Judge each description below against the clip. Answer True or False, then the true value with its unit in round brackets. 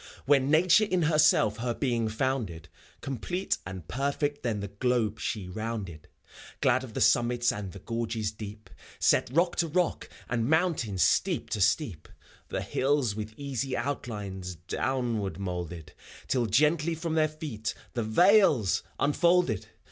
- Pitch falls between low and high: False (120 Hz)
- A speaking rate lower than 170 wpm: True (140 wpm)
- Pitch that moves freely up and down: True (5.8 semitones)